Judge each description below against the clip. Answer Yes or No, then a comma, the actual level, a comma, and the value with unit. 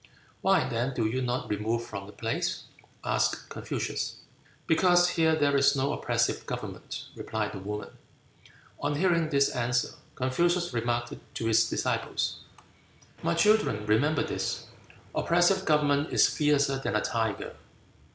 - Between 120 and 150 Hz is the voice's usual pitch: Yes, low, 135 Hz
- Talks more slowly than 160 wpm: Yes, slow, 135 wpm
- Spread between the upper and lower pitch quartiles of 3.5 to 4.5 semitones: No, wide, 5.5 semitones